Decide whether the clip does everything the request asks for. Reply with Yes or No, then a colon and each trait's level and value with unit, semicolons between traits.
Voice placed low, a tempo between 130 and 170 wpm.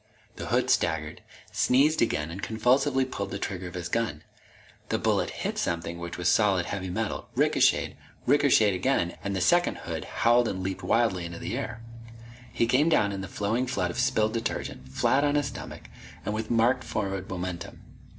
No: low, 105 Hz; average, 180 wpm